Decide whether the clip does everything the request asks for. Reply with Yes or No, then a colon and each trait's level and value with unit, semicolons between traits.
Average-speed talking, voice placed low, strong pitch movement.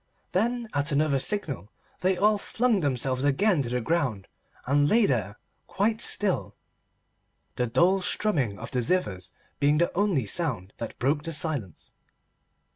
No: average, 145 wpm; medium, 145 Hz; wide, 7.5 semitones